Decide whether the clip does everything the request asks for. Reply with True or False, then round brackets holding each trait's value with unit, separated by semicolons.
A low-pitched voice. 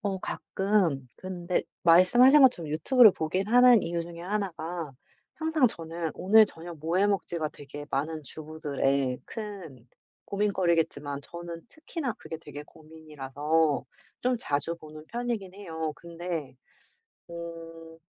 False (170 Hz)